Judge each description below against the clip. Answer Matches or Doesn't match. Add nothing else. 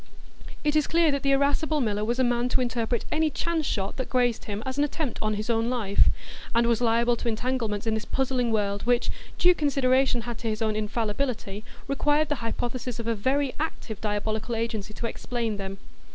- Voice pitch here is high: Matches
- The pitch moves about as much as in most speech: Matches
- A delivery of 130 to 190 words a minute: Doesn't match